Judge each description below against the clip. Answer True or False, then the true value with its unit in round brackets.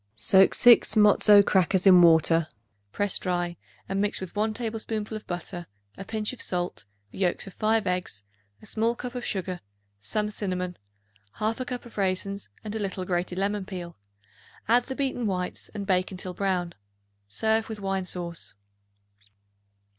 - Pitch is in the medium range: False (195 Hz)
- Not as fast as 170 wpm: True (160 wpm)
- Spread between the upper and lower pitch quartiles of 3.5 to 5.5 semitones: False (3.1 semitones)